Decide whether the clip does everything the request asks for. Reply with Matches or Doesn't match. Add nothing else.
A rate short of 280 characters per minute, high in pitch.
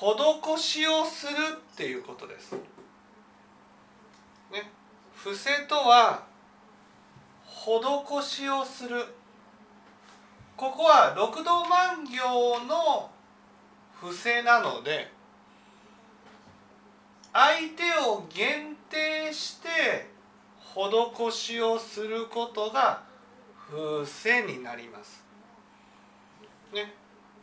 Matches